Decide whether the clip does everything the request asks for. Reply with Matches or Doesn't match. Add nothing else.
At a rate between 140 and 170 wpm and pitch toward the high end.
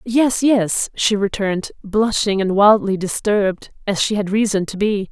Matches